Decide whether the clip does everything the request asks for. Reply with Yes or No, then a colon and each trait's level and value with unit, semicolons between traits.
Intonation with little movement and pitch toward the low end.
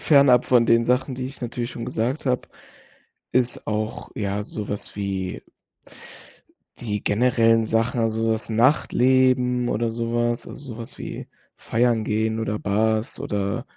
Yes: narrow, 2.3 semitones; low, 115 Hz